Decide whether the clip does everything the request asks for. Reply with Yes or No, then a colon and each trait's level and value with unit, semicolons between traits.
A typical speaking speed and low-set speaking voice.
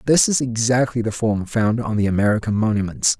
Yes: average, 190 wpm; low, 115 Hz